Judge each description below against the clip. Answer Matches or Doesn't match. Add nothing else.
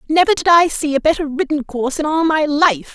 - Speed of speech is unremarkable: Doesn't match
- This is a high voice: Matches